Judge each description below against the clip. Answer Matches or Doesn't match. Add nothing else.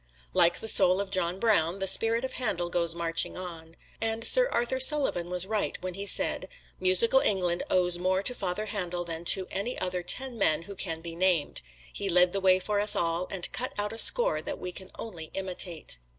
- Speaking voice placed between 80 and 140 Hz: Doesn't match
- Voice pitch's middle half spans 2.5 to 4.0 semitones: Matches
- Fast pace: Matches